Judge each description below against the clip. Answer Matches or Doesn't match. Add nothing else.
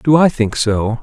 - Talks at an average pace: Doesn't match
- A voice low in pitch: Matches